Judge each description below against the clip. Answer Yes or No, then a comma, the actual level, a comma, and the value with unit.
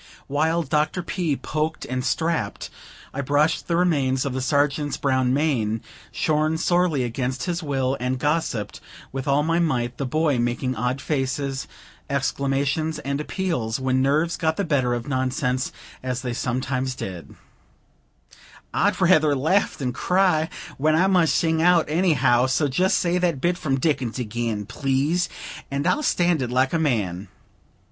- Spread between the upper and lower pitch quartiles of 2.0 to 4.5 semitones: Yes, average, 4.0 semitones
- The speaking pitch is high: No, medium, 140 Hz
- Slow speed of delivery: No, average, 155 wpm